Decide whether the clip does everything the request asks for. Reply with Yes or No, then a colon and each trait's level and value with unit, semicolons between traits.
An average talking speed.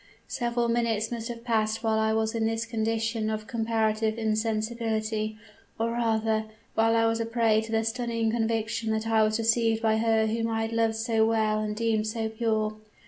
Yes: average, 190 wpm